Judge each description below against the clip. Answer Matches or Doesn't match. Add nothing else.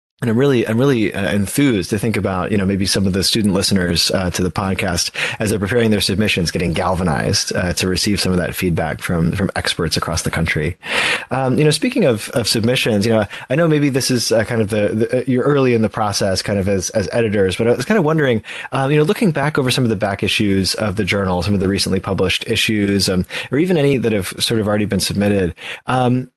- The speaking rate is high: Matches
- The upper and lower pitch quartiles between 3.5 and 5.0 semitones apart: Matches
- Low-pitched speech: Matches